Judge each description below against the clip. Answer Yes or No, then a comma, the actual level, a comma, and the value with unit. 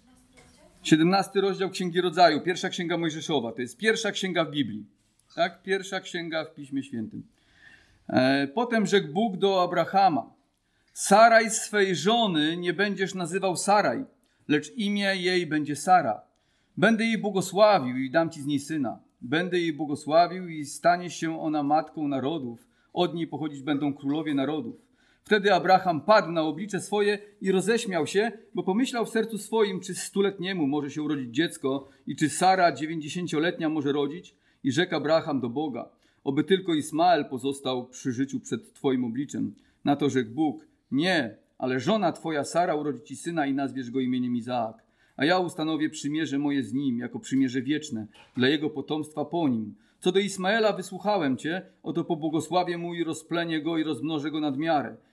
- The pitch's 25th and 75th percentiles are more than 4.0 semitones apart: Yes, average, 5.0 semitones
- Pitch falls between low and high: Yes, medium, 165 Hz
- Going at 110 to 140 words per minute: No, fast, 160 wpm